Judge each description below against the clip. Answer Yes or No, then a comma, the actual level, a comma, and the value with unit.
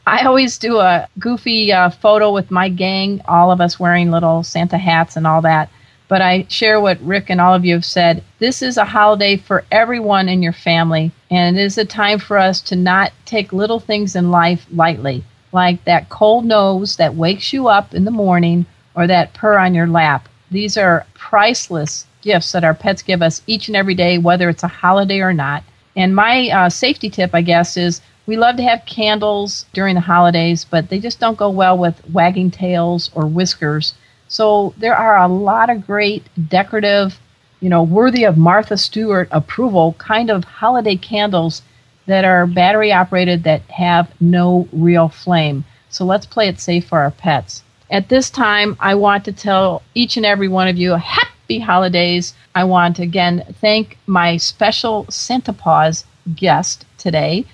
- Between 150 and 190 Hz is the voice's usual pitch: Yes, medium, 185 Hz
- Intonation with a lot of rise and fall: No, average, 3.4 semitones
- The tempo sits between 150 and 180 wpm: No, average, 190 wpm